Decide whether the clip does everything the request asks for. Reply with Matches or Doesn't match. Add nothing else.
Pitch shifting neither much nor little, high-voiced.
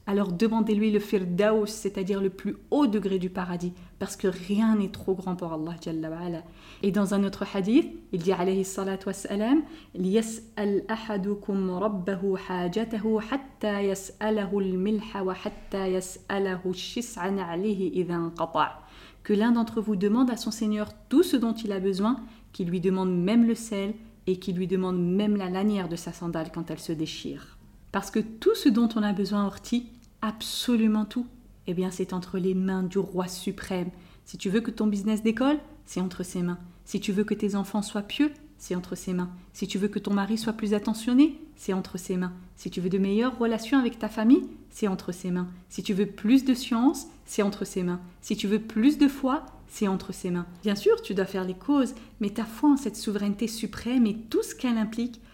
Matches